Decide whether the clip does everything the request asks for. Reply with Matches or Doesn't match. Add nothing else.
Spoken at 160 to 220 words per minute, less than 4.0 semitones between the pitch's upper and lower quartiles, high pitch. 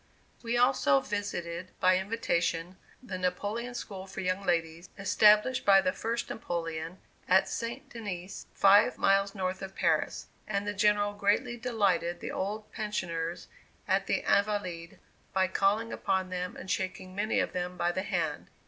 Doesn't match